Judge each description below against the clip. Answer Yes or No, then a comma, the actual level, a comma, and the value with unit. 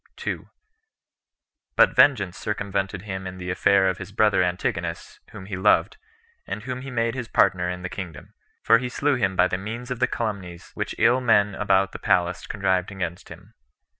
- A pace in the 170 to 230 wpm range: Yes, average, 185 wpm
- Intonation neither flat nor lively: Yes, average, 3.8 semitones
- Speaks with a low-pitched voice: Yes, low, 100 Hz